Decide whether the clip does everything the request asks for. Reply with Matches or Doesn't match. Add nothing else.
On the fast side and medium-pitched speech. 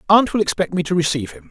Matches